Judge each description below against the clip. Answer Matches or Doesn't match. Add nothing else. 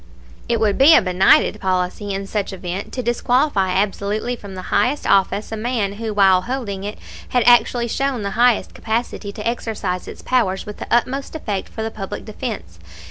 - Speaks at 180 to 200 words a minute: Matches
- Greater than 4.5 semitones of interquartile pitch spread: Doesn't match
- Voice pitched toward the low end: Doesn't match